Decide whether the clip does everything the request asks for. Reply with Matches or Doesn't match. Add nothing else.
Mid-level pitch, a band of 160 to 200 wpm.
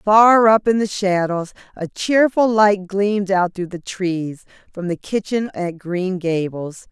Doesn't match